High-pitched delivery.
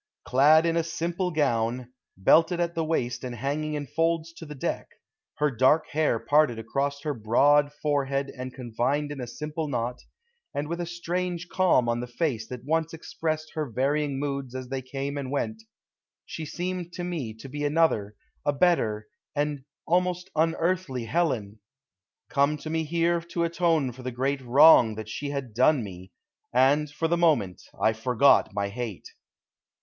No: medium, 145 Hz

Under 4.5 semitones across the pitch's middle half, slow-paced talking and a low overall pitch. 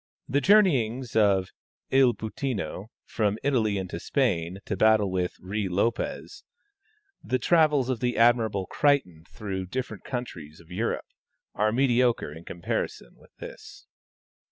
No: average, 5.2 semitones; slow, 130 wpm; low, 110 Hz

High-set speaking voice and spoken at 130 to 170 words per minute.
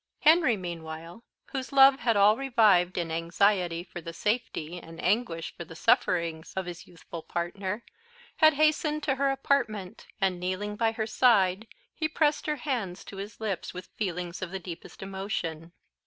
Yes: high, 195 Hz; average, 165 wpm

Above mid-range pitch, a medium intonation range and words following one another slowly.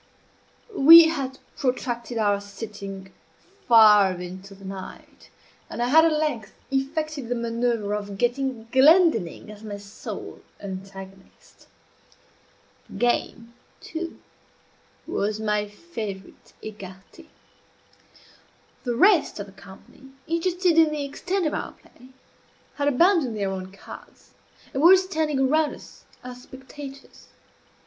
No: high, 240 Hz; wide, 6.9 semitones; slow, 120 wpm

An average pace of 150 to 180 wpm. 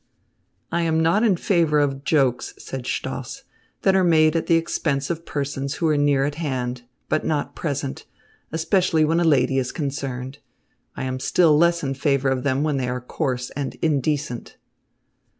Yes: average, 175 wpm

